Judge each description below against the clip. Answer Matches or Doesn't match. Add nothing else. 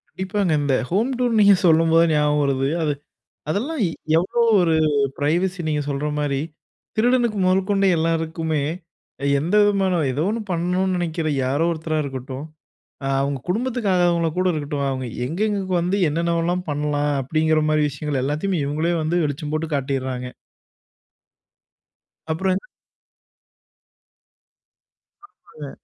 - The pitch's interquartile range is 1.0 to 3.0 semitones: Doesn't match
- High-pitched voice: Doesn't match